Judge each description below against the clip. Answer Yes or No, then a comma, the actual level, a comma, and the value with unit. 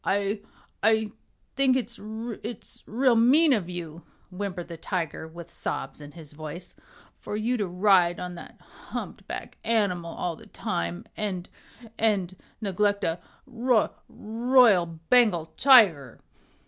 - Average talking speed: No, slow, 130 wpm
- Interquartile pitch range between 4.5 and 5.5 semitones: Yes, average, 4.8 semitones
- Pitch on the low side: No, high, 195 Hz